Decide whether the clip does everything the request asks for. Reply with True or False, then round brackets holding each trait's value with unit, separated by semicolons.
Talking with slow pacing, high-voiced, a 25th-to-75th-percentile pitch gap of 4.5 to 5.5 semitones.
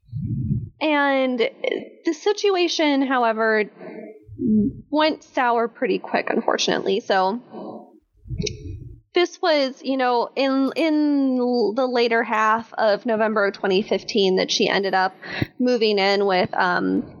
True (110 wpm; 245 Hz; 5.2 semitones)